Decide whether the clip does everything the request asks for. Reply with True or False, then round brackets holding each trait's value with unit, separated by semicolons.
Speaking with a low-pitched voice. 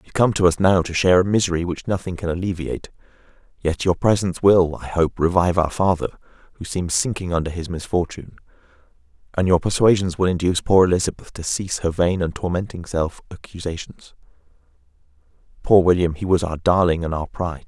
True (90 Hz)